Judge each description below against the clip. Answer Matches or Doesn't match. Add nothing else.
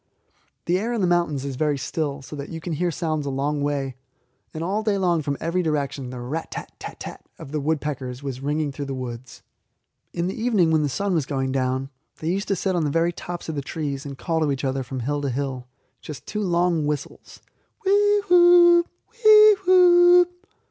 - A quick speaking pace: Matches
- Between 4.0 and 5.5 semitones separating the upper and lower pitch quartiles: Matches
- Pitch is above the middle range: Doesn't match